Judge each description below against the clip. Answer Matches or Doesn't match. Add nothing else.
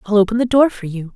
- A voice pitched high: Matches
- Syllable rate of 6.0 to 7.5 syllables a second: Matches